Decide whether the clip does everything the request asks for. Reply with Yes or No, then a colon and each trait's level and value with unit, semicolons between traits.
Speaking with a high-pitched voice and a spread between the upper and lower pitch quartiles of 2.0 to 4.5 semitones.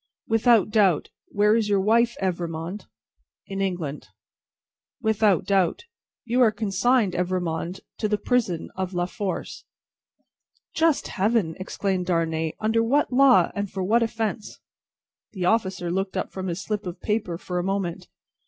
Yes: high, 195 Hz; average, 3.6 semitones